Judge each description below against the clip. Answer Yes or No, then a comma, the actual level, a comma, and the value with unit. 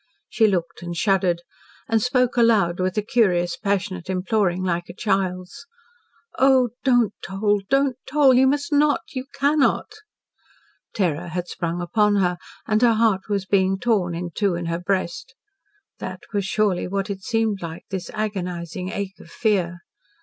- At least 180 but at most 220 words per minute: No, average, 155 wpm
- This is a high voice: Yes, high, 195 Hz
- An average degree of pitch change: Yes, average, 4.2 semitones